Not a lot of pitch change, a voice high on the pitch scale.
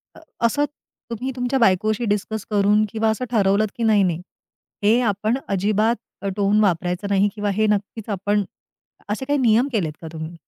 Yes: narrow, 2.3 semitones; high, 210 Hz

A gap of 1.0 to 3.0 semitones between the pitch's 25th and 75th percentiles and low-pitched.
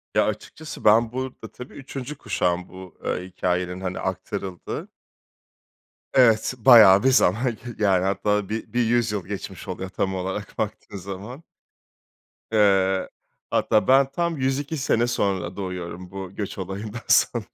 No: average, 4.3 semitones; low, 105 Hz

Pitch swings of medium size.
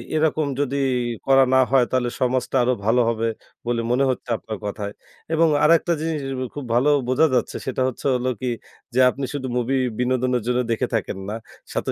No: narrow, 2.2 semitones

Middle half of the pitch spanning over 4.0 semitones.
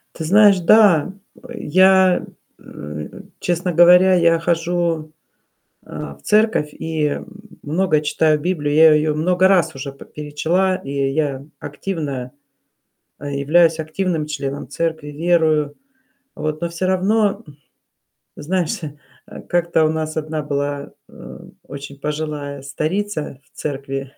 No: average, 3.4 semitones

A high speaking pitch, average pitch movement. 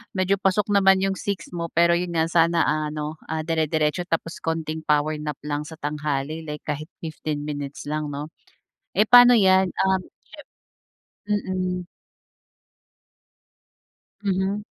No: medium, 165 Hz; average, 3.8 semitones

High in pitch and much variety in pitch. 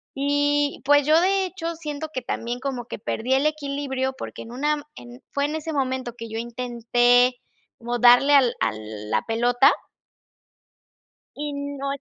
No: very high, 265 Hz; average, 3.2 semitones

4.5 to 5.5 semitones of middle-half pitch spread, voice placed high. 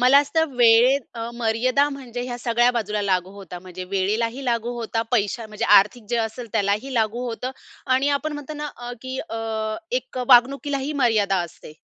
No: average, 3.2 semitones; high, 240 Hz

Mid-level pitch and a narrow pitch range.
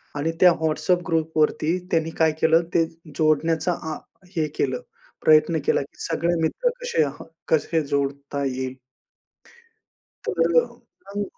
Yes: medium, 160 Hz; narrow, 1.8 semitones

